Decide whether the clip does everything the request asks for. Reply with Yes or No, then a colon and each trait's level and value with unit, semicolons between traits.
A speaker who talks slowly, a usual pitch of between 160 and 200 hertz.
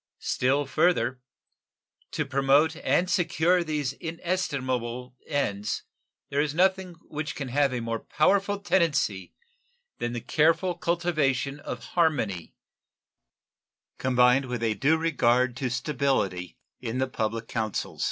No: slow, 120 wpm; medium, 140 Hz